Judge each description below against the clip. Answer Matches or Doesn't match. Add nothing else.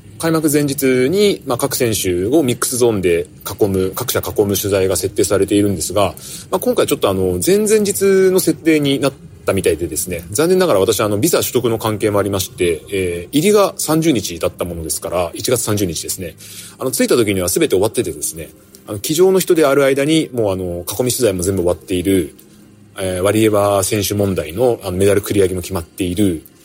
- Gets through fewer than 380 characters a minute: Doesn't match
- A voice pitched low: Matches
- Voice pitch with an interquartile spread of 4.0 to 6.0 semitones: Doesn't match